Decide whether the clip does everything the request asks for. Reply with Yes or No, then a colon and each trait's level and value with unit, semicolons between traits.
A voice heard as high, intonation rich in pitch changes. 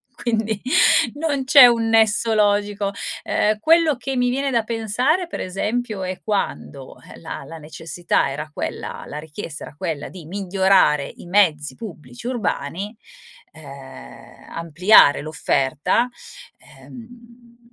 Yes: high, 205 Hz; wide, 6.8 semitones